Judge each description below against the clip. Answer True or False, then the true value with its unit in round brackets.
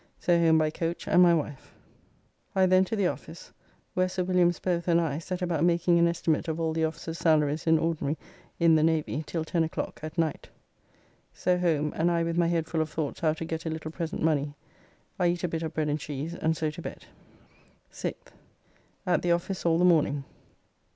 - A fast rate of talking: True (210 wpm)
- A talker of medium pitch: True (165 Hz)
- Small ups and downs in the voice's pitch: True (1.7 semitones)